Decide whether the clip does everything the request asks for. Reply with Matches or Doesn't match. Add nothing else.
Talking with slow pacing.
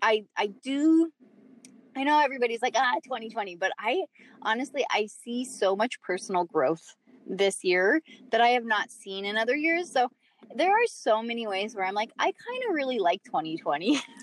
Doesn't match